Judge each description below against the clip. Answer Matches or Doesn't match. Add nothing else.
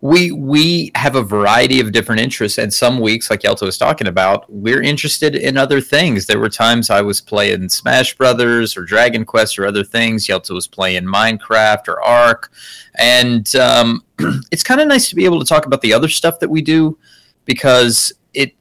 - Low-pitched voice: Matches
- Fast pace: Doesn't match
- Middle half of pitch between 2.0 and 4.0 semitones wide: Doesn't match